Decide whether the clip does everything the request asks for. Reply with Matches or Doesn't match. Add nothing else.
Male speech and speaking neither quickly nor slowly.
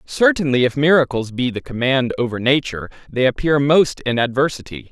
Matches